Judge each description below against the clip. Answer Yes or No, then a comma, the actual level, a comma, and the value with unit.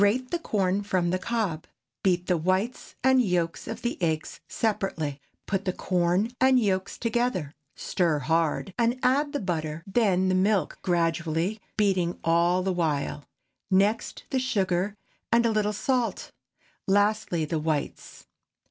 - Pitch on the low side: No, high, 190 Hz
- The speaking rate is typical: Yes, average, 145 wpm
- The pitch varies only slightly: No, average, 4.3 semitones